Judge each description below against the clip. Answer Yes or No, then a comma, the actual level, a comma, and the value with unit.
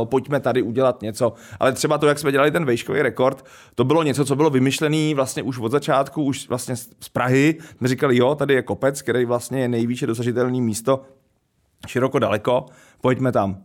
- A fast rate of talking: Yes, fast, 195 wpm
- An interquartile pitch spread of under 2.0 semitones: No, narrow, 2.5 semitones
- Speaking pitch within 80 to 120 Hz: No, low, 130 Hz